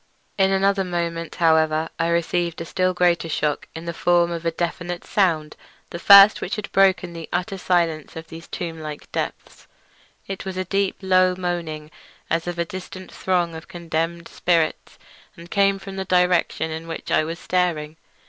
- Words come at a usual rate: Yes, average, 175 wpm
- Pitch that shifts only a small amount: Yes, narrow, 2.0 semitones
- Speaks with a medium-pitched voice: Yes, medium, 170 Hz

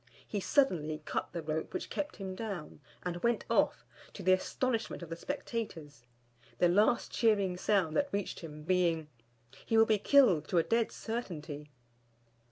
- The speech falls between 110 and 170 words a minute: Yes, average, 165 wpm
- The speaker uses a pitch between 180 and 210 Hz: Yes, medium, 185 Hz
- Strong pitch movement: Yes, wide, 5.7 semitones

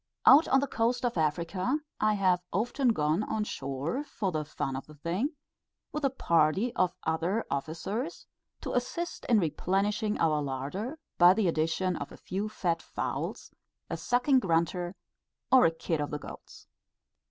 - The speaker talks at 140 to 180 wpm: Yes, average, 165 wpm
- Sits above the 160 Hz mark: Yes, medium, 185 Hz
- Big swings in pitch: Yes, wide, 6.6 semitones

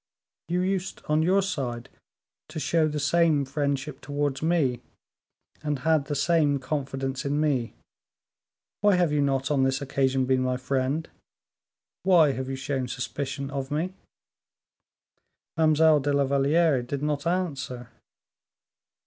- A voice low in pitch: No, medium, 145 Hz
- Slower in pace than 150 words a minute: Yes, slow, 135 wpm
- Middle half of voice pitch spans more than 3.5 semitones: No, average, 3.0 semitones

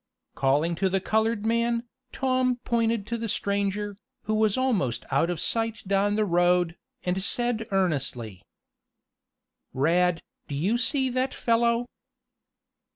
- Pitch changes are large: No, average, 4.8 semitones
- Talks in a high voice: Yes, high, 205 Hz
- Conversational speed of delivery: No, slow, 130 wpm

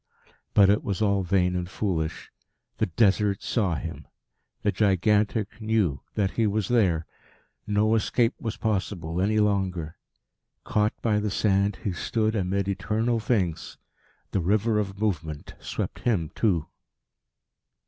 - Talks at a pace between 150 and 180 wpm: No, slow, 135 wpm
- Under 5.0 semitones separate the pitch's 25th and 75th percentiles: Yes, average, 2.9 semitones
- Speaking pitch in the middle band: No, low, 100 Hz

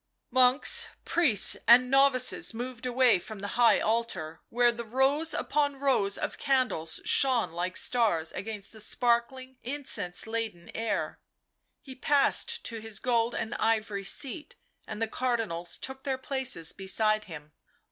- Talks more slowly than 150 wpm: Yes, average, 140 wpm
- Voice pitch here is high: Yes, high, 235 Hz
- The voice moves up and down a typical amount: Yes, average, 3.6 semitones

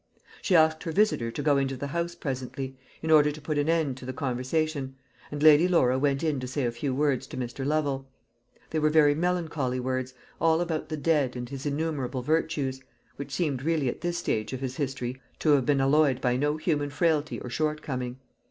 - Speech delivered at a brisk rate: Yes, fast, 210 wpm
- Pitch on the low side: No, medium, 145 Hz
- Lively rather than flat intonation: No, average, 3.2 semitones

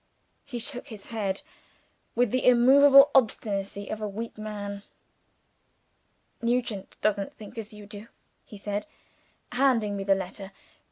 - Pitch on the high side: Yes, high, 215 Hz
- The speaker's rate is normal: No, slow, 130 wpm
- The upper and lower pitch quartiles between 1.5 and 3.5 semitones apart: Yes, average, 3.2 semitones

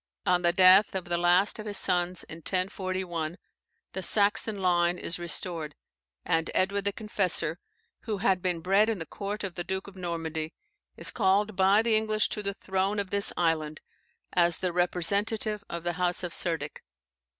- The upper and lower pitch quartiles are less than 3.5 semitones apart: Yes, average, 2.7 semitones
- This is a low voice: No, medium, 185 Hz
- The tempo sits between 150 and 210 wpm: Yes, average, 175 wpm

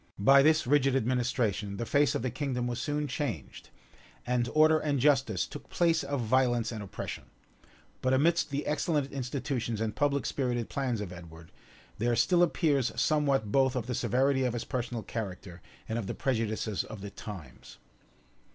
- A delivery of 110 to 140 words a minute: No, average, 170 wpm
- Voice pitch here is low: Yes, low, 125 Hz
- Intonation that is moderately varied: Yes, average, 4.1 semitones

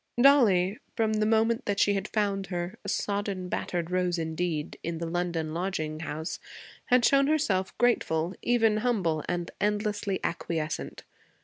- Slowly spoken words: No, average, 145 wpm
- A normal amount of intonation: Yes, average, 4.2 semitones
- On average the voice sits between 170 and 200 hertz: Yes, high, 190 Hz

